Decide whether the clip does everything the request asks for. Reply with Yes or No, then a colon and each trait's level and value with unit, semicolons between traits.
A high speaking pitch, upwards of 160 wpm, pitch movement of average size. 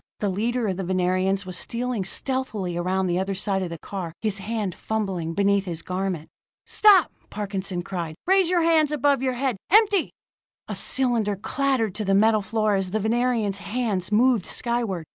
Yes: high, 205 Hz; average, 175 wpm; average, 4.6 semitones